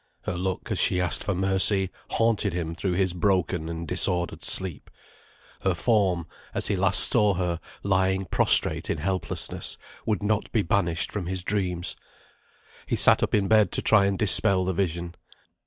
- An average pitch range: No, narrow, 2.2 semitones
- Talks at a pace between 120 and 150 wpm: No, average, 170 wpm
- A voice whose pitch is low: Yes, very low, 95 Hz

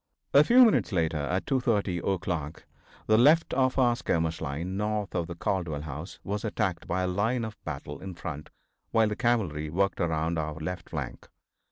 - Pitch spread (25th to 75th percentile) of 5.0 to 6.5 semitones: Yes, wide, 5.4 semitones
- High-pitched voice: No, very low, 90 Hz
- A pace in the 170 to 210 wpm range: Yes, average, 180 wpm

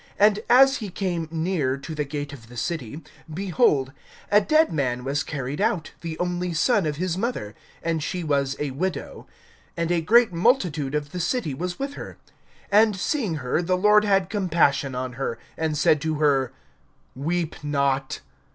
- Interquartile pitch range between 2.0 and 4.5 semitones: No, average, 5.1 semitones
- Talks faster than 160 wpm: Yes, average, 175 wpm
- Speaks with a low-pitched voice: No, medium, 165 Hz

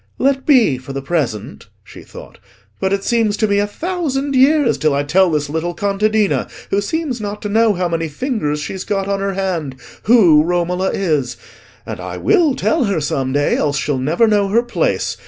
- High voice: Yes, high, 195 Hz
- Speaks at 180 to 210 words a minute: Yes, average, 195 wpm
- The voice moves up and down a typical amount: No, wide, 7.0 semitones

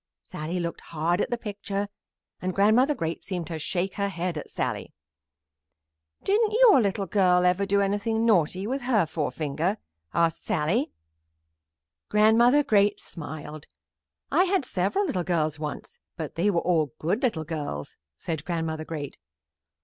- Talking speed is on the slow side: No, average, 145 wpm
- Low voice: No, medium, 185 Hz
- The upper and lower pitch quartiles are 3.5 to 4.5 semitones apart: No, average, 4.9 semitones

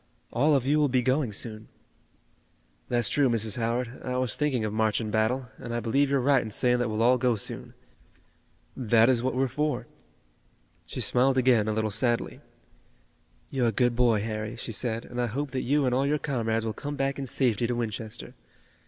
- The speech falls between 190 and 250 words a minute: Yes, fast, 205 wpm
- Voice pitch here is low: Yes, low, 120 Hz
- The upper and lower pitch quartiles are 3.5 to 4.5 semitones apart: No, average, 2.8 semitones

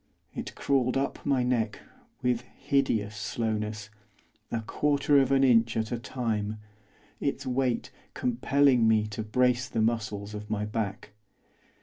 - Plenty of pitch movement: No, average, 2.9 semitones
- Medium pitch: No, low, 115 Hz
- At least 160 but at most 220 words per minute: No, slow, 135 wpm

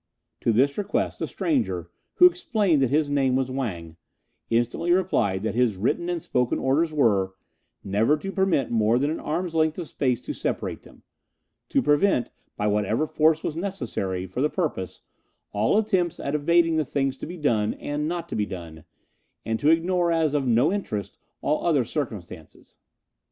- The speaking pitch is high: No, medium, 145 Hz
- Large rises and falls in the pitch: Yes, wide, 7.1 semitones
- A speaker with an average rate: Yes, average, 175 wpm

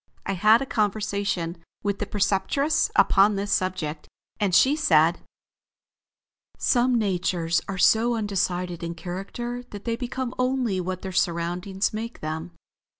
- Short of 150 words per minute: Yes, slow, 135 wpm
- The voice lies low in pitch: No, high, 195 Hz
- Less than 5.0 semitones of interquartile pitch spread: Yes, average, 4.4 semitones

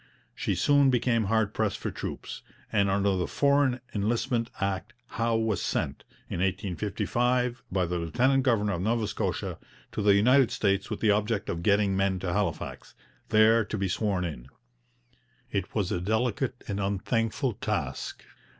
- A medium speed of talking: Yes, average, 160 wpm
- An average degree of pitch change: Yes, average, 3.3 semitones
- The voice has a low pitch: Yes, low, 105 Hz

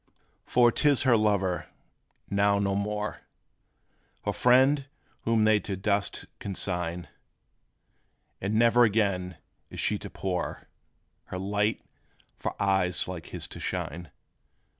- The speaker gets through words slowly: Yes, slow, 120 wpm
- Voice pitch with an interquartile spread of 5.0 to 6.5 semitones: No, average, 3.2 semitones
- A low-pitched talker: Yes, low, 100 Hz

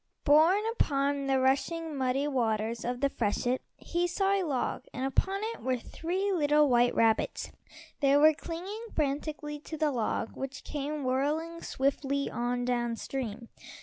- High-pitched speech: Yes, very high, 280 Hz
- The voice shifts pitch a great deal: No, average, 3.9 semitones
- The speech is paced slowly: No, average, 150 wpm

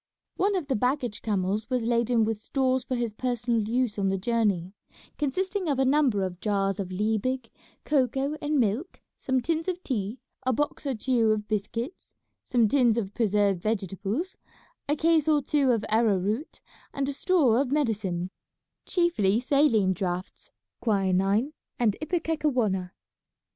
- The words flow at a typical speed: Yes, average, 155 wpm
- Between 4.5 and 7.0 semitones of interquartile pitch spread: Yes, average, 5.3 semitones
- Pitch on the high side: Yes, high, 235 Hz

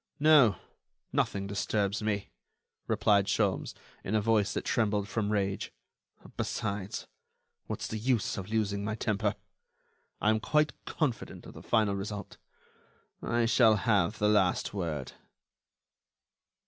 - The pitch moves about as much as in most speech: No, narrow, 1.8 semitones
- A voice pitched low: Yes, low, 105 Hz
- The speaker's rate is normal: No, slow, 125 wpm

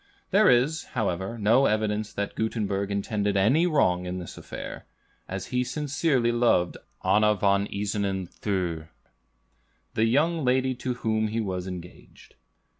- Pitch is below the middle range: Yes, low, 105 Hz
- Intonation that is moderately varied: Yes, average, 4.4 semitones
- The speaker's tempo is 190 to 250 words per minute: No, slow, 135 wpm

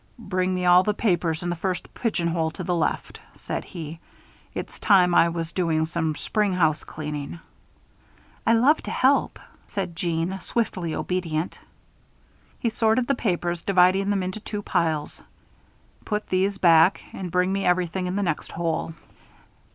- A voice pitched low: No, medium, 180 Hz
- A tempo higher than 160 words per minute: No, average, 155 wpm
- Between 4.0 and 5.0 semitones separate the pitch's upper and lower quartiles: No, average, 3.0 semitones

